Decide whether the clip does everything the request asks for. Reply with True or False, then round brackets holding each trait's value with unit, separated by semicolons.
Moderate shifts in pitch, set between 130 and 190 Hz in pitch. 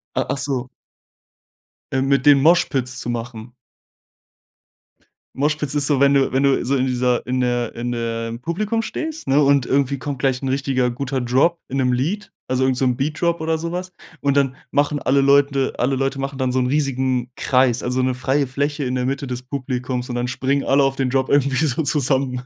False (2.0 semitones; 135 Hz)